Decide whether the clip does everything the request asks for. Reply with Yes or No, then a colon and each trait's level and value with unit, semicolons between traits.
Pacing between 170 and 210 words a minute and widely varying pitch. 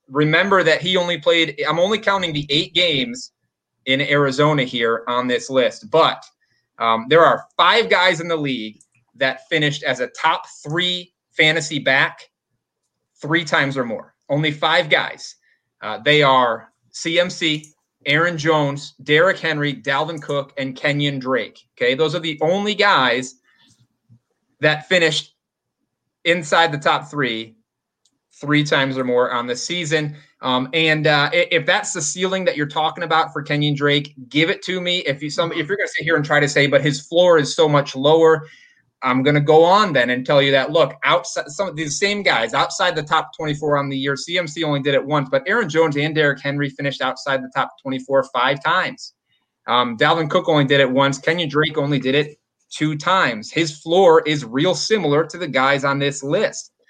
No: average, 190 wpm; average, 3.2 semitones